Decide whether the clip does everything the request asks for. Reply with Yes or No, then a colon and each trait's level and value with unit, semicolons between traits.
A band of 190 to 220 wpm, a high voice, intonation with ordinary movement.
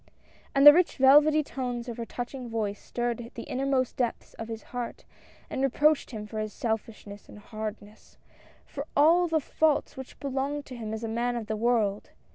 Yes: average, 195 wpm; high, 240 Hz; average, 3.7 semitones